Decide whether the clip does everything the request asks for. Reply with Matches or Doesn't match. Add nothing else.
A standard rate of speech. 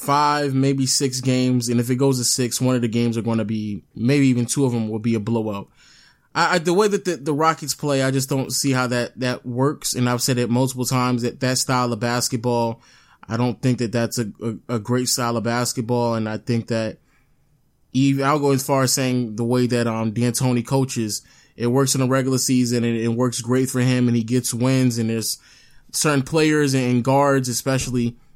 Doesn't match